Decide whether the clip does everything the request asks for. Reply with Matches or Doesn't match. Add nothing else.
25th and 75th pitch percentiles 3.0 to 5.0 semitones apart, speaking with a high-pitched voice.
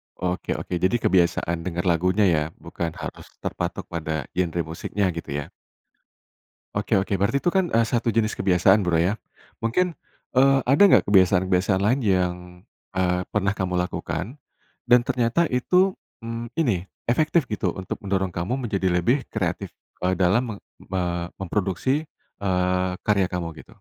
Doesn't match